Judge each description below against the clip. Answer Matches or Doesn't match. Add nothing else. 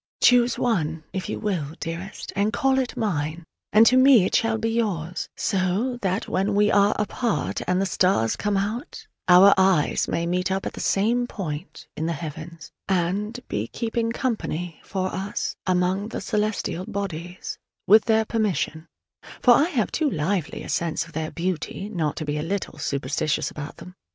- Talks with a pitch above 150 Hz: Matches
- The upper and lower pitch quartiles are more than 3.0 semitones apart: Matches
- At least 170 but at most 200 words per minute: Matches